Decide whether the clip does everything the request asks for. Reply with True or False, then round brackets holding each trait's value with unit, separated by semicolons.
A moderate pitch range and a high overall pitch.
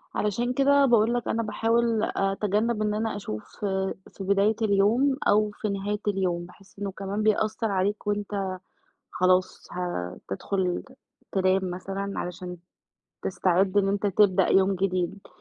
False (2.3 semitones; 200 Hz)